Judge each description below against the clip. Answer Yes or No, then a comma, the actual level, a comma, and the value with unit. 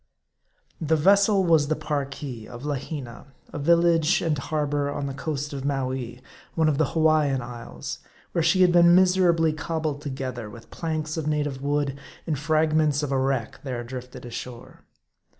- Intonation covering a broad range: No, average, 3.2 semitones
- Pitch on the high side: No, medium, 145 Hz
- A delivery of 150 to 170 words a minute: Yes, average, 165 wpm